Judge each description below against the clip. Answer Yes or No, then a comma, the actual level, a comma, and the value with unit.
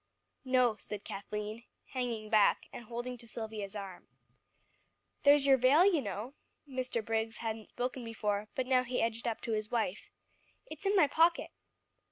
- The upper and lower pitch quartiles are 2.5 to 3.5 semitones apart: Yes, average, 3.1 semitones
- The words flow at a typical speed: Yes, average, 160 wpm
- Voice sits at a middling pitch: No, high, 235 Hz